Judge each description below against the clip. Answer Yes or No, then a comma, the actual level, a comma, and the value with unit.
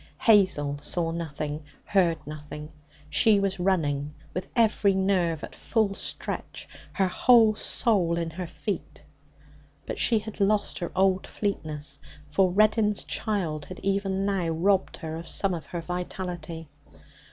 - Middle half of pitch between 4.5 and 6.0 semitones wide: No, average, 3.6 semitones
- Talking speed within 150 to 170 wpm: No, average, 140 wpm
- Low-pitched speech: No, medium, 185 Hz